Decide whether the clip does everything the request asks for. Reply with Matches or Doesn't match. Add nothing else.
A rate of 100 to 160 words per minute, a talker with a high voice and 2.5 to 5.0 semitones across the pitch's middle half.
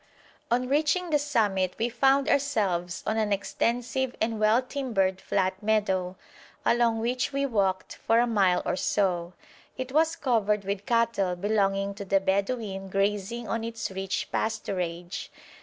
Matches